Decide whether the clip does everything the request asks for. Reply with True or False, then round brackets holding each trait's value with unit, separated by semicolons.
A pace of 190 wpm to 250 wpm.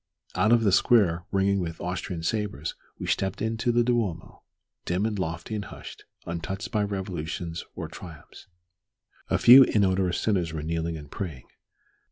False (155 wpm)